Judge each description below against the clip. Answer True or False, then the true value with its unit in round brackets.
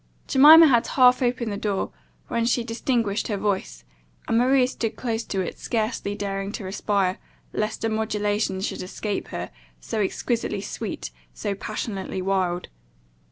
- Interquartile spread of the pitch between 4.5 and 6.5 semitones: False (3.2 semitones)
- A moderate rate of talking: True (150 wpm)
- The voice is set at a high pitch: True (210 Hz)